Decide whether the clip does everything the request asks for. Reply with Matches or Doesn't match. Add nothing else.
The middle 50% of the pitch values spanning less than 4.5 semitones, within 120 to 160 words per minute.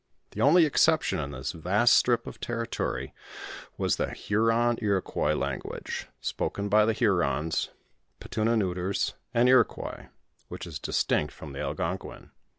Doesn't match